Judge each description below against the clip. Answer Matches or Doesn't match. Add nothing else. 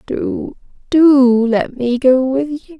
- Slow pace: Matches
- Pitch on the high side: Matches